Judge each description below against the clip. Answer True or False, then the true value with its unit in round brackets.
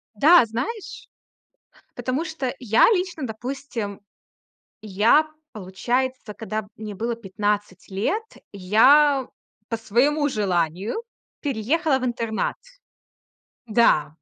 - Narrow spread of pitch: False (5.1 semitones)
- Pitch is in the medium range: False (230 Hz)